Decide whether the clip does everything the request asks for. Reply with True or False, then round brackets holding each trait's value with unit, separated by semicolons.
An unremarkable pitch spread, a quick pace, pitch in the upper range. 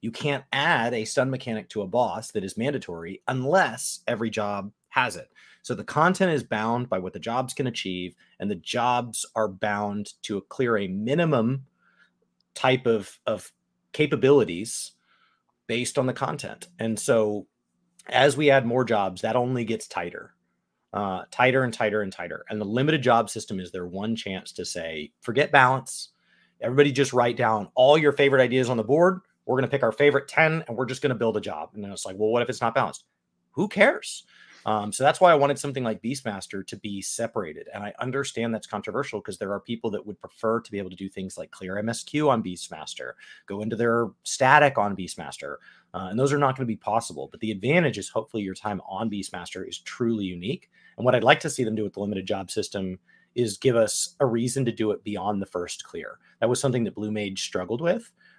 False (4.6 semitones; 215 wpm; 115 Hz)